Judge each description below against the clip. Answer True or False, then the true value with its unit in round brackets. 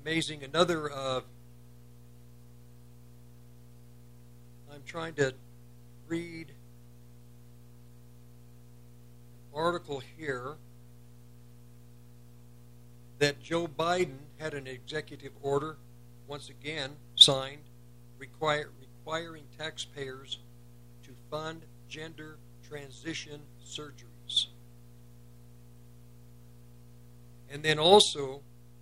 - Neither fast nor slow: False (65 wpm)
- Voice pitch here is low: True (120 Hz)